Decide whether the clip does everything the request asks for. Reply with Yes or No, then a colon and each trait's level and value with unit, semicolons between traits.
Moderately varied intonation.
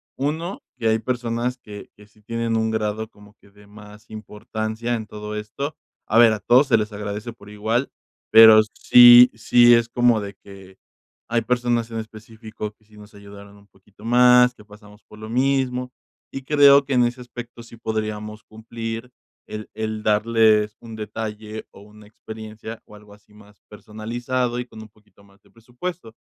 No: narrow, 2.2 semitones